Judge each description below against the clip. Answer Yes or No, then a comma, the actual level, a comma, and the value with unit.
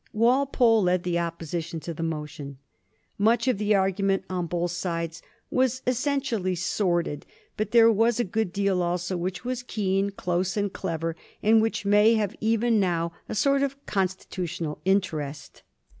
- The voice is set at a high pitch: Yes, high, 195 Hz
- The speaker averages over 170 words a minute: No, average, 160 wpm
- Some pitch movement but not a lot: Yes, average, 4.5 semitones